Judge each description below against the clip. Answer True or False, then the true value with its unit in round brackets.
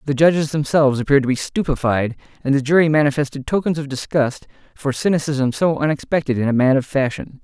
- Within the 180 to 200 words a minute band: True (185 wpm)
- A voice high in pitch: False (140 Hz)